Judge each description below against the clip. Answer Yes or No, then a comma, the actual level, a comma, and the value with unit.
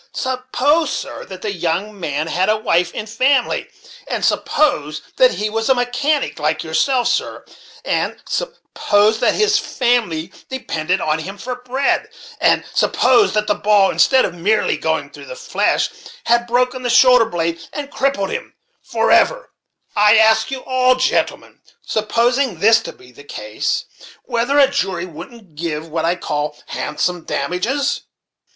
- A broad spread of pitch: Yes, wide, 6.9 semitones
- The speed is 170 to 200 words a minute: No, average, 155 wpm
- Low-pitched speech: No, high, 220 Hz